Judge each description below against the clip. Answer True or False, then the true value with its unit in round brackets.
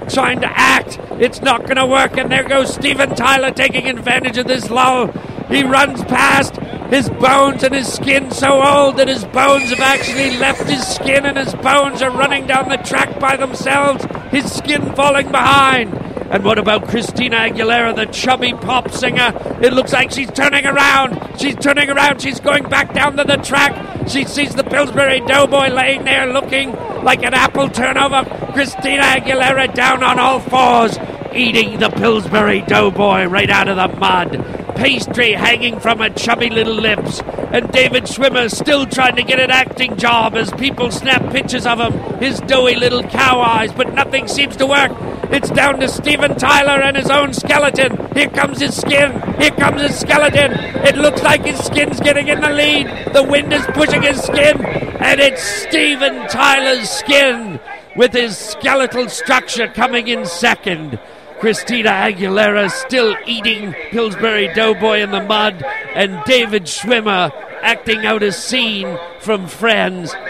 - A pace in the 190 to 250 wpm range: False (165 wpm)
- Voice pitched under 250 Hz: False (255 Hz)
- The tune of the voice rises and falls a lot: False (3.3 semitones)